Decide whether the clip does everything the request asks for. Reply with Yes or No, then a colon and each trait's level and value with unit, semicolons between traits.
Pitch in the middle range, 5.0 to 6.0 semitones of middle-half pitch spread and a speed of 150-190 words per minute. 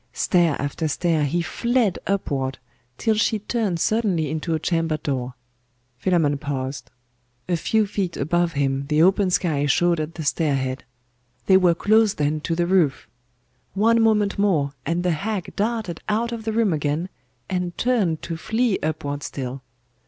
Yes: medium, 170 Hz; wide, 5.6 semitones; average, 160 wpm